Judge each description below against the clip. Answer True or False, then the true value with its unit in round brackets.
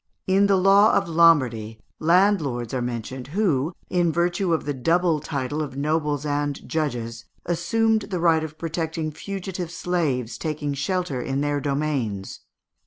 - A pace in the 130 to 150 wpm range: True (145 wpm)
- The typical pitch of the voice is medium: True (155 Hz)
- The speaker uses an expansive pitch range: False (4.3 semitones)